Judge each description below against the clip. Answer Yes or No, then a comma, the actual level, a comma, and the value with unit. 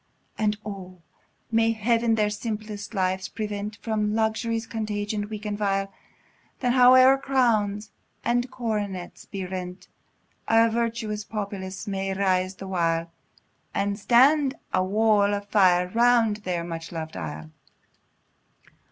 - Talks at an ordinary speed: No, slow, 125 wpm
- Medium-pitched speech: No, high, 210 Hz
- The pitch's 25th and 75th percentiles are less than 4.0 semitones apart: Yes, average, 2.9 semitones